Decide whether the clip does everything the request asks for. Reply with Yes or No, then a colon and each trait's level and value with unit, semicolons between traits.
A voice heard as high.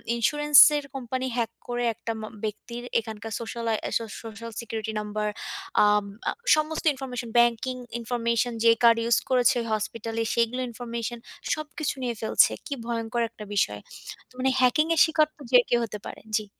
Yes: high, 235 Hz